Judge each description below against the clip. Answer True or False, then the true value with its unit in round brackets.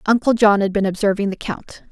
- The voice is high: True (205 Hz)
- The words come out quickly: True (220 wpm)